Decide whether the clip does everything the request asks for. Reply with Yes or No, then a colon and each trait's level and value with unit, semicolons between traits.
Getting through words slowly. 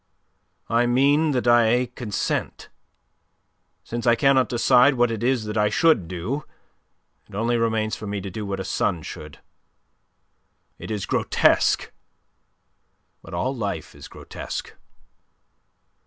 Yes: slow, 130 wpm